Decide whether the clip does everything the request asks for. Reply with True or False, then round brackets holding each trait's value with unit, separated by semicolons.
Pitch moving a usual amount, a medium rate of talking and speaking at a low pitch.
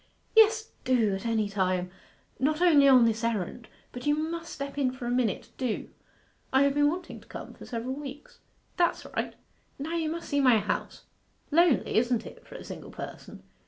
False (4.8 semitones; 190 wpm; 265 Hz)